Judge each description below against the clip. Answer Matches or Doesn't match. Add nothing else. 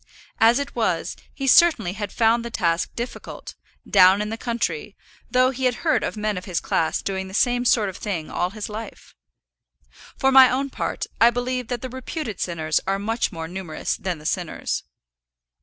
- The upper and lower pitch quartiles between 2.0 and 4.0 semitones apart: Doesn't match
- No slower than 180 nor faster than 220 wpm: Matches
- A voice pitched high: Matches